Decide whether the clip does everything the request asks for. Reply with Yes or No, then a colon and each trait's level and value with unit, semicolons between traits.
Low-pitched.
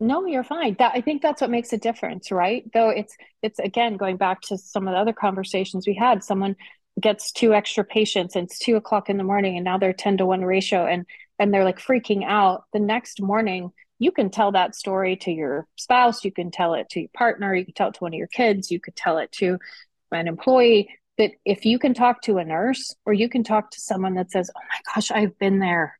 No: high, 205 Hz